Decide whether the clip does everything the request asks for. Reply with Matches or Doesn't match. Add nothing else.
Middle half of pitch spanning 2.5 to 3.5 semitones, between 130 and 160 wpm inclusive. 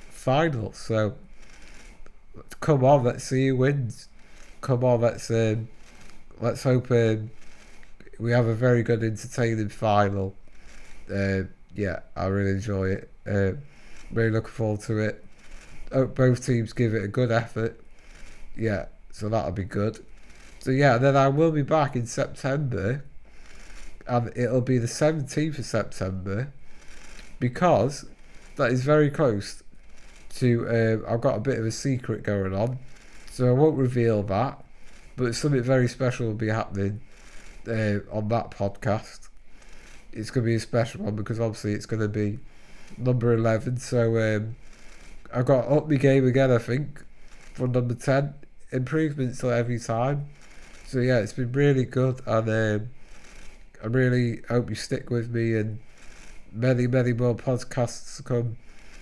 Matches